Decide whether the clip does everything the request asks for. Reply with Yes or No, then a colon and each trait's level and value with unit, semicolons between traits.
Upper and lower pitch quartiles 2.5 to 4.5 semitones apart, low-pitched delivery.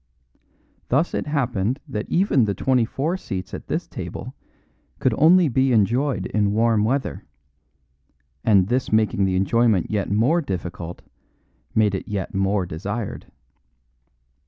No: average, 5.2 semitones; low, 110 Hz